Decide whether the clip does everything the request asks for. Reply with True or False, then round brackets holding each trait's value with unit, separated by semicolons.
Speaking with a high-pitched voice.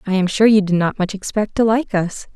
True (200 Hz)